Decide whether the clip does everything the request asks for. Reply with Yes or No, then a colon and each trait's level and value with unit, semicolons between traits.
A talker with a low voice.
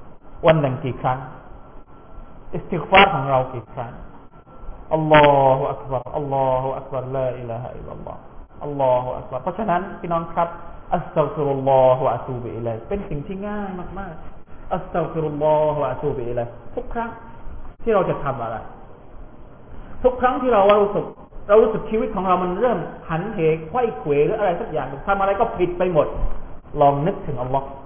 No: medium, 150 Hz